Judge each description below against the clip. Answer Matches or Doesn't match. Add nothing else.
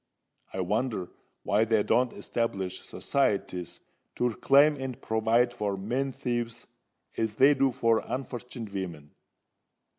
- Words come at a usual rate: Doesn't match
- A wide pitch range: Doesn't match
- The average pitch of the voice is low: Matches